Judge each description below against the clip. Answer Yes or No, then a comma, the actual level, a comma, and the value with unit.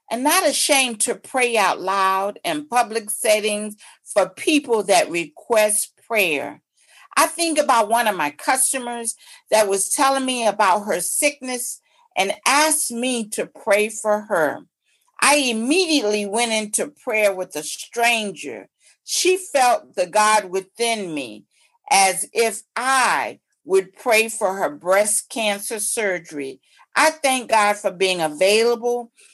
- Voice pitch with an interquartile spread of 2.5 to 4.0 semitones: No, average, 4.9 semitones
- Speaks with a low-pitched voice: No, high, 230 Hz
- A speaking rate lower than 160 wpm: Yes, slow, 135 wpm